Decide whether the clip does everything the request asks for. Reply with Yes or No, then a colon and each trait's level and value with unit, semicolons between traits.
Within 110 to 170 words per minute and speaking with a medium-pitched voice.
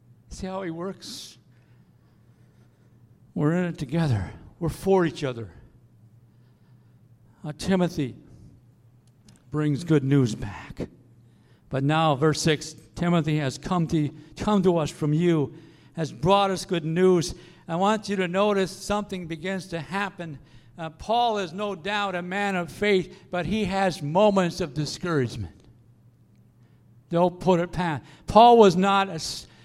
Yes: average, 140 wpm; medium, 155 Hz